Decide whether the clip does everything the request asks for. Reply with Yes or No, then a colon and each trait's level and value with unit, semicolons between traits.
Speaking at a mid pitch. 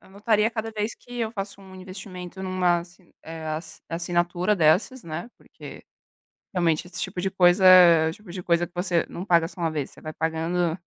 Yes: medium, 180 Hz